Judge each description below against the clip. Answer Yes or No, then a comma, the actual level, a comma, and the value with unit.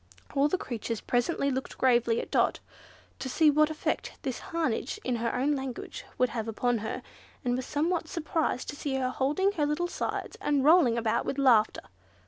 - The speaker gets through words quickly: No, average, 185 wpm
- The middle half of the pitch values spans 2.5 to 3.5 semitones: No, average, 3.9 semitones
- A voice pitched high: Yes, very high, 265 Hz